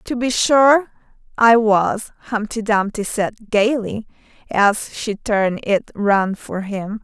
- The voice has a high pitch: Yes, high, 215 Hz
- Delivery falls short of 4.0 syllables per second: Yes, 3.5 syllables/s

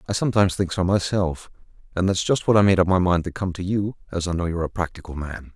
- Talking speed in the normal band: No, fast, 270 wpm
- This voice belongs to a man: Yes, male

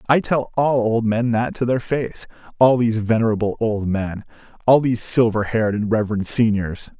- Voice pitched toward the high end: No, low, 115 Hz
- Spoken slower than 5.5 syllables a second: Yes, 5.2 syllables/s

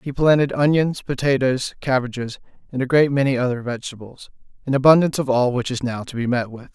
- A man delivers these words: Yes, male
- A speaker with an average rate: Yes, average, 195 wpm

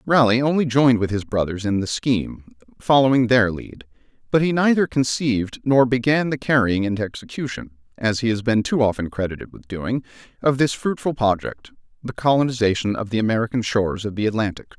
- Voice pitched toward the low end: Yes, low, 115 Hz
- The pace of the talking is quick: No, average, 170 wpm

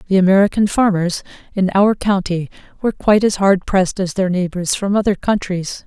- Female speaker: Yes, female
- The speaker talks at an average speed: Yes, average, 175 wpm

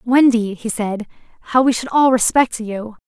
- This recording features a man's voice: No, female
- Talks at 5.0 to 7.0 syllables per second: No, 4.6 syllables/s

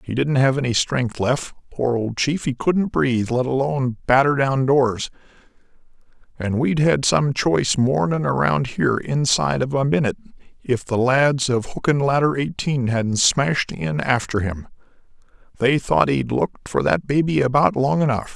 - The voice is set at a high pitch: No, low, 130 Hz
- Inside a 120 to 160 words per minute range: No, average, 170 wpm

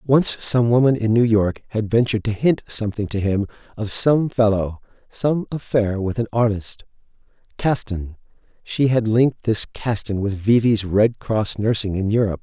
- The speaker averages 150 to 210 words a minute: Yes, average, 170 wpm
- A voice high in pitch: No, low, 110 Hz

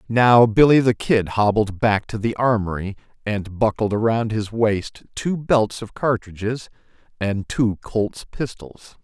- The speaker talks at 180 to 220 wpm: No, average, 145 wpm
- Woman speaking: No, male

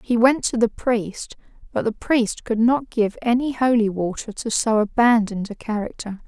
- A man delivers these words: No, female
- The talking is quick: No, average, 180 wpm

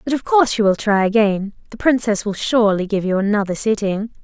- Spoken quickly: Yes, fast, 215 wpm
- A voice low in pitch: No, high, 215 Hz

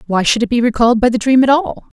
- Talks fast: Yes, fast, 300 wpm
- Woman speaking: Yes, female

